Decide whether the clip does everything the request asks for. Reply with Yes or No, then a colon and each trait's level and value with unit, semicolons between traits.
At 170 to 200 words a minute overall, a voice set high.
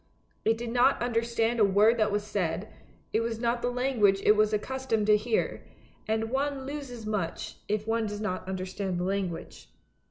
Yes: average, 180 wpm; high, 220 Hz